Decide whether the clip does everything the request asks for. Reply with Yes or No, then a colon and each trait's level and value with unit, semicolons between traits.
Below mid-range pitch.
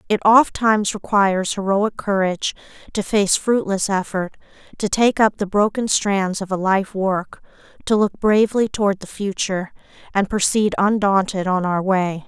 No: high, 200 Hz